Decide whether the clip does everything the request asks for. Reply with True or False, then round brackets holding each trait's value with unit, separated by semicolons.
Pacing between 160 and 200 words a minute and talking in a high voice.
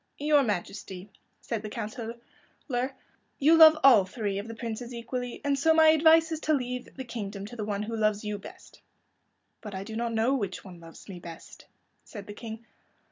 True (190 wpm; 230 Hz)